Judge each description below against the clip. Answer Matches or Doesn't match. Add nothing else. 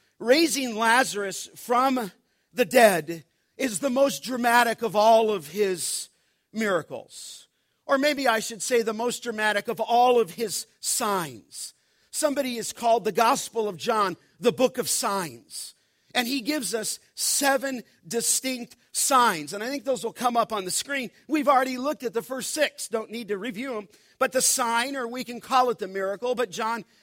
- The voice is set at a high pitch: Matches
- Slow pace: Doesn't match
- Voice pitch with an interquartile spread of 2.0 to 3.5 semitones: Matches